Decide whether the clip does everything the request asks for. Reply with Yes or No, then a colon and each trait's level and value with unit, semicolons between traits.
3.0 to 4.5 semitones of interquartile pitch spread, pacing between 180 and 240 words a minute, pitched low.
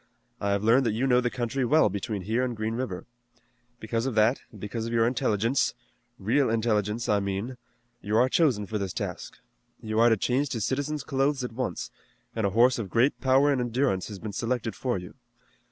Yes: average, 3.3 semitones; fast, 205 wpm; low, 115 Hz